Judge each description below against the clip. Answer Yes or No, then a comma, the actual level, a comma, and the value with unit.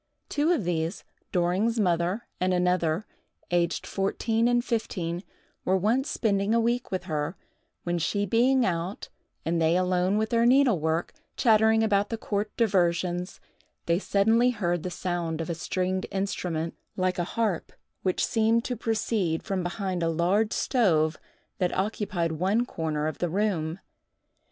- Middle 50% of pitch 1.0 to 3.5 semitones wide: No, average, 4.3 semitones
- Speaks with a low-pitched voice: No, medium, 185 Hz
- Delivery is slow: No, average, 150 wpm